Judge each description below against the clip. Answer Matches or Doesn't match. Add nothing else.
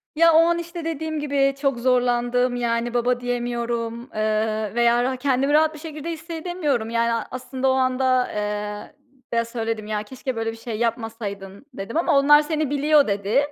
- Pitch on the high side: Matches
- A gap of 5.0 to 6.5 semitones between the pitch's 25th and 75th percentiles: Doesn't match